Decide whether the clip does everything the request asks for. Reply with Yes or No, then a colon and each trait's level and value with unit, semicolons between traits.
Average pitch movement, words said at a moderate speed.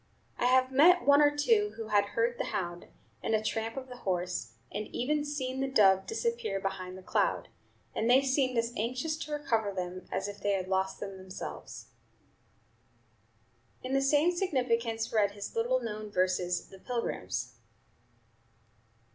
No: wide, 5.7 semitones; average, 165 wpm